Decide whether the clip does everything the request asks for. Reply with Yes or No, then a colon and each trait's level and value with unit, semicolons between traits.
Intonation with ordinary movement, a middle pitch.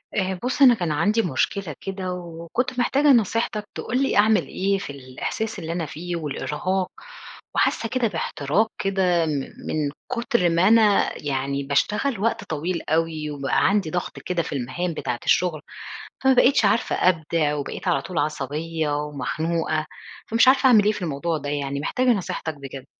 No: wide, 5.8 semitones; medium, 175 Hz